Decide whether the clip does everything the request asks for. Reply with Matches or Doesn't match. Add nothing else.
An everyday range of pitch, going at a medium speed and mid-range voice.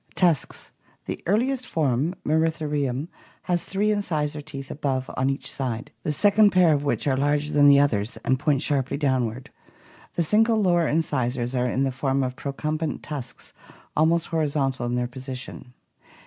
Matches